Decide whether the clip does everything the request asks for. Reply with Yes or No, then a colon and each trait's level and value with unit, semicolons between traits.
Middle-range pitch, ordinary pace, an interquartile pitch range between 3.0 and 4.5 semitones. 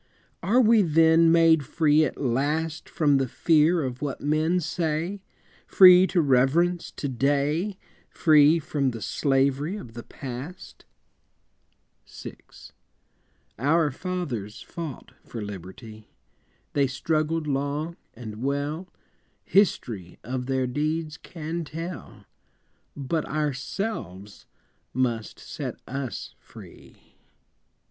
No: medium, 150 Hz; slow, 105 wpm; average, 4.1 semitones